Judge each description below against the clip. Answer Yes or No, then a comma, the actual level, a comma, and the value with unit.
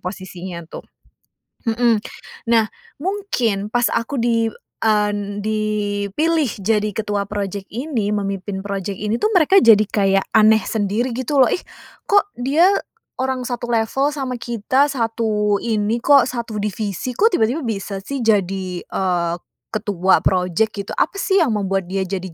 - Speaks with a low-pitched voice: No, high, 215 Hz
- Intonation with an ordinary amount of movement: Yes, average, 3.7 semitones